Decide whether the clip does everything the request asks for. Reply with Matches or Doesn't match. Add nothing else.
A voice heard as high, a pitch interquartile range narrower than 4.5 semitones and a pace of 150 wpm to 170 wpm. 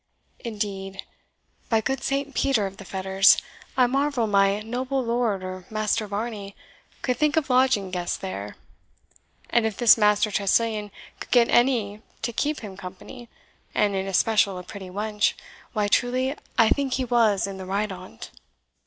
Matches